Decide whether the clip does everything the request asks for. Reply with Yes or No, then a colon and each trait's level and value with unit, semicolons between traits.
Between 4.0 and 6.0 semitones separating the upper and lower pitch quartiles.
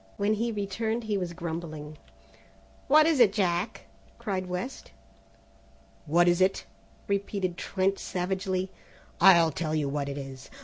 No: average, 3.2 semitones